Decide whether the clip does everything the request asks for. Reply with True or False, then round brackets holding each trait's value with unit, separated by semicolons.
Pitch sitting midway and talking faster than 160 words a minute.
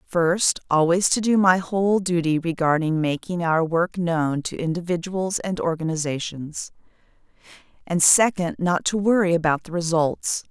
False (170 Hz; 135 wpm)